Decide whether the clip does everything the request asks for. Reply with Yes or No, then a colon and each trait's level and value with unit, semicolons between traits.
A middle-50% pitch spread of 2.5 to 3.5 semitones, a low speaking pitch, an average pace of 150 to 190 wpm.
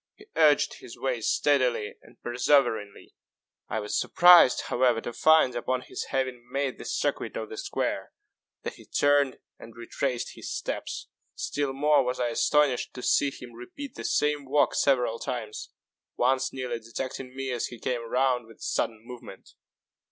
Yes: average, 2.9 semitones; low, 130 Hz; average, 165 wpm